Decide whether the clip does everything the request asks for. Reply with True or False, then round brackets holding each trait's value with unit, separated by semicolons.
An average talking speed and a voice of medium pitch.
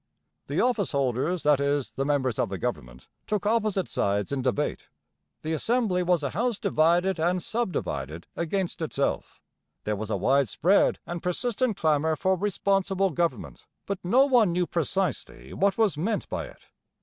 True (165 wpm; 175 Hz)